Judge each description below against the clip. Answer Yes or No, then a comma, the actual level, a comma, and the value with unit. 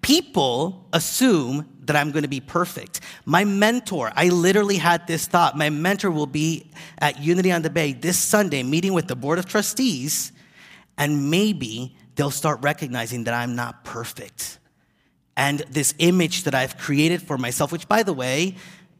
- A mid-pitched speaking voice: Yes, medium, 165 Hz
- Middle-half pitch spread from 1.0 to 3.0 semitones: No, average, 3.8 semitones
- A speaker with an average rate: Yes, average, 165 wpm